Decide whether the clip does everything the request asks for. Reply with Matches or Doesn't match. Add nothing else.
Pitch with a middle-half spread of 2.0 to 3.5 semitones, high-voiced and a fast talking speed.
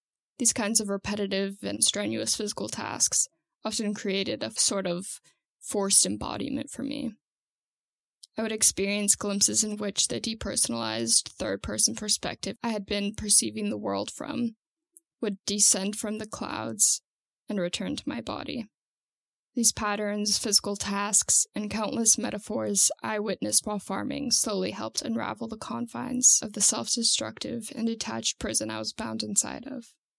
Doesn't match